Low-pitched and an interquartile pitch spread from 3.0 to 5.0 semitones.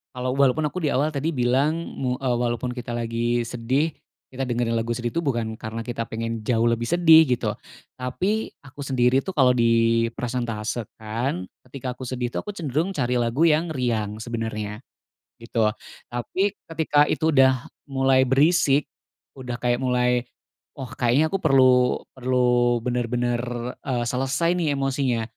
No: low, 125 Hz; narrow, 2.6 semitones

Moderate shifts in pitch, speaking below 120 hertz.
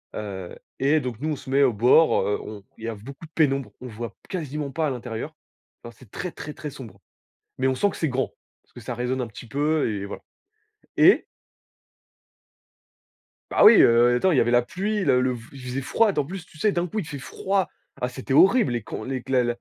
No: average, 4.4 semitones; low, 130 Hz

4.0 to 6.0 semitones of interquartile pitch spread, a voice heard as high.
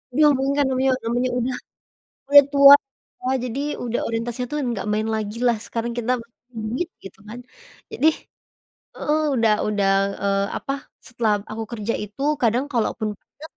No: average, 3.3 semitones; high, 240 Hz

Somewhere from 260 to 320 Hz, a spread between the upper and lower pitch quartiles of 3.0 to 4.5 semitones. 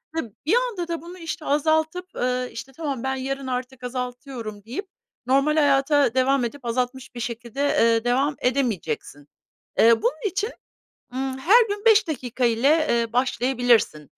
Yes: very high, 265 Hz; average, 3.9 semitones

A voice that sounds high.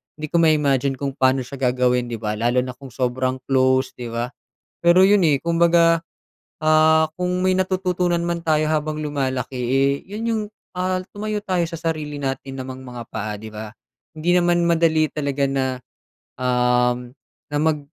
No: medium, 145 Hz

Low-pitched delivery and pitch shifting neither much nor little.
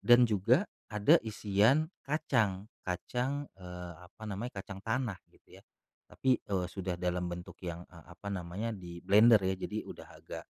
Yes: low, 100 Hz; average, 4.7 semitones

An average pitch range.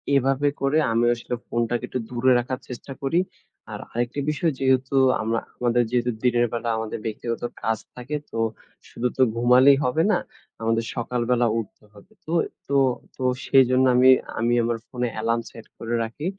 No: narrow, 2.0 semitones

